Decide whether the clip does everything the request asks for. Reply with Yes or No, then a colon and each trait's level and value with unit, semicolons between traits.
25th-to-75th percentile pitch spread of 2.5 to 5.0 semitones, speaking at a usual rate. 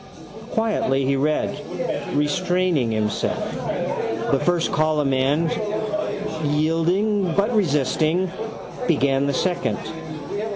No: average, 4.6 semitones; slow, 85 wpm